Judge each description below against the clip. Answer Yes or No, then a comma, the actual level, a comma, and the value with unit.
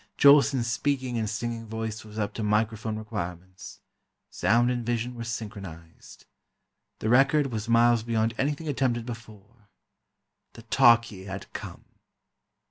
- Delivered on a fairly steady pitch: Yes, narrow, 2.2 semitones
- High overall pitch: No, low, 115 Hz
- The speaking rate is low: Yes, slow, 125 wpm